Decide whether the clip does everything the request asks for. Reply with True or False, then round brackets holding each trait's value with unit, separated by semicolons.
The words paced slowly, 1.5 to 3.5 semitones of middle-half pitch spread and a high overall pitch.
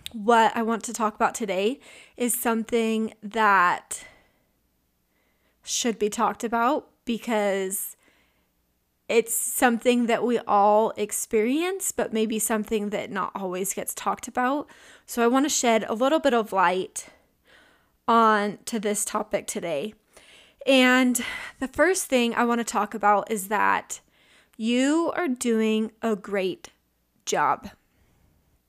True (130 wpm; 2.8 semitones; 225 Hz)